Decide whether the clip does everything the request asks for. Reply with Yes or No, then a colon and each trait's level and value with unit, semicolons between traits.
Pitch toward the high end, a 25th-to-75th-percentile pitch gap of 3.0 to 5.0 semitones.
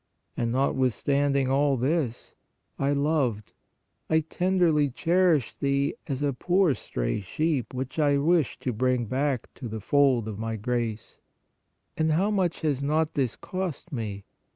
No: medium, 140 Hz; average, 4.4 semitones